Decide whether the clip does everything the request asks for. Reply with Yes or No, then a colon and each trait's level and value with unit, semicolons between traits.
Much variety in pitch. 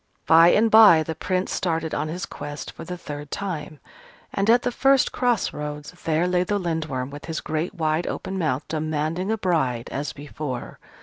No: average, 3.7 semitones